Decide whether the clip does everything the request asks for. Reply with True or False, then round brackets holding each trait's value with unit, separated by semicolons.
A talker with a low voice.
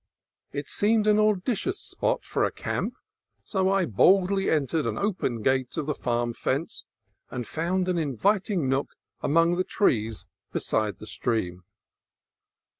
False (160 Hz)